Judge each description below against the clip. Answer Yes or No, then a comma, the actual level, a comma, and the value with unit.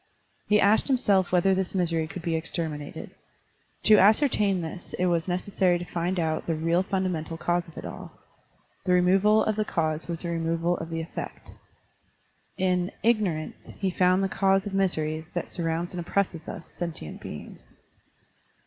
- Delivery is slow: No, average, 165 wpm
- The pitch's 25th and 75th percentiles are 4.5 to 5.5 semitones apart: No, average, 2.7 semitones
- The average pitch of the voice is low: No, medium, 175 Hz